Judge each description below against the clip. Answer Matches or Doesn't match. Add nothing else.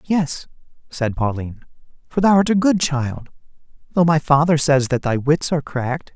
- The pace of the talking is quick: Doesn't match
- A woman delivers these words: Doesn't match